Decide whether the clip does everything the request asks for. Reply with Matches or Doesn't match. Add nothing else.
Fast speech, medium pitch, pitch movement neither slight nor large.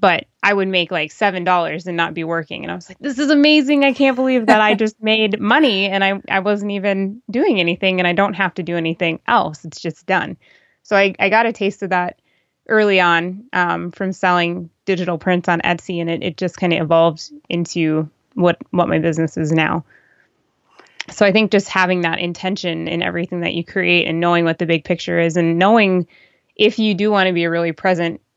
Matches